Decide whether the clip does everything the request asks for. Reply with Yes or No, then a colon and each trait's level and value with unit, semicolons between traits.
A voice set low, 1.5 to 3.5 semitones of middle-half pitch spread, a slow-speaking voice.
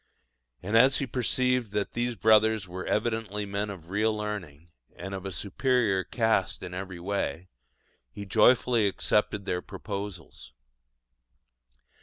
Yes: low, 105 Hz; average, 2.9 semitones; slow, 130 wpm